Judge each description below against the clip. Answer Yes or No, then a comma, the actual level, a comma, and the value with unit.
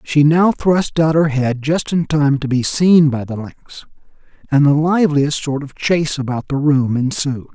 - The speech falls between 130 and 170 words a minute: No, average, 200 wpm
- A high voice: No, medium, 145 Hz